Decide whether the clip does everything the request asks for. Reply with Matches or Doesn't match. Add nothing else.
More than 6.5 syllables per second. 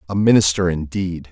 Doesn't match